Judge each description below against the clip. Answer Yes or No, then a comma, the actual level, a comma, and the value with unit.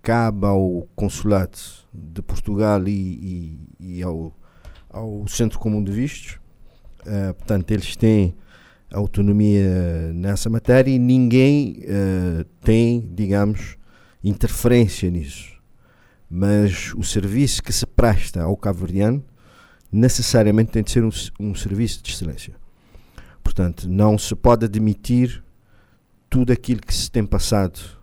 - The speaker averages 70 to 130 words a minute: Yes, slow, 120 wpm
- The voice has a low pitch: Yes, low, 105 Hz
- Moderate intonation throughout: Yes, average, 3.6 semitones